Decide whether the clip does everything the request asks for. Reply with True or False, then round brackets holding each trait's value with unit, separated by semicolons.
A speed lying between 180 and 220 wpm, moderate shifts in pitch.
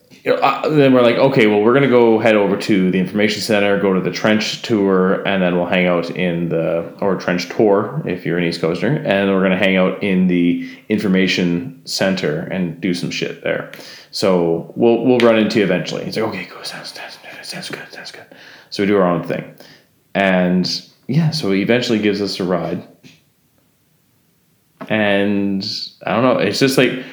True (200 wpm; 3.4 semitones)